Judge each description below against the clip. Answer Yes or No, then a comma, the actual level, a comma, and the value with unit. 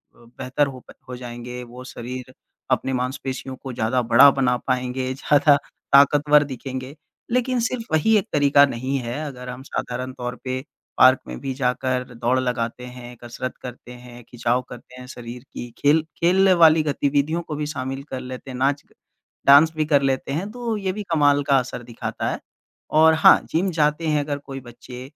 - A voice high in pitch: No, low, 130 Hz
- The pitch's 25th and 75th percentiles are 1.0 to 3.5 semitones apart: Yes, average, 2.9 semitones